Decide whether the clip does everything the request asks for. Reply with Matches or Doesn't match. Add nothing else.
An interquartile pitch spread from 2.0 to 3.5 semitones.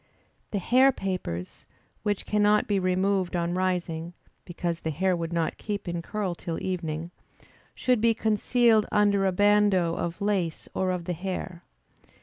Matches